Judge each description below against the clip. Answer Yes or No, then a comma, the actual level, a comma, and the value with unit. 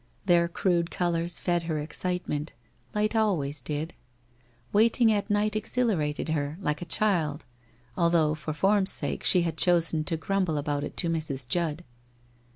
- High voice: No, medium, 170 Hz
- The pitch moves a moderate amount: Yes, average, 4.1 semitones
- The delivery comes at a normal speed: Yes, average, 160 wpm